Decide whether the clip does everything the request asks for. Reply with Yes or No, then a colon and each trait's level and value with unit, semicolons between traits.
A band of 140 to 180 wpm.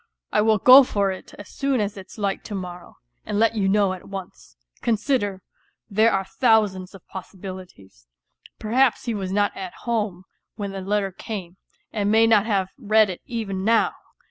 Yes: average, 175 wpm